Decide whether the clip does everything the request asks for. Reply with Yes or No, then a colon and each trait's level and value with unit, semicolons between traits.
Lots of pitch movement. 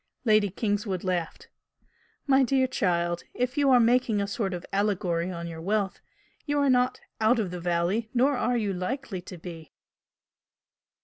Yes: wide, 5.8 semitones